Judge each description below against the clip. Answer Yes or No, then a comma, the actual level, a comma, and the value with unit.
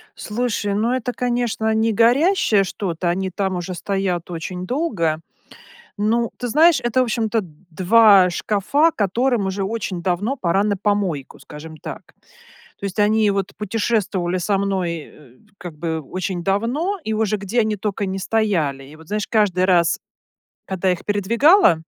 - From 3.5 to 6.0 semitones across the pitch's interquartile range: Yes, average, 3.9 semitones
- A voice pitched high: Yes, high, 200 Hz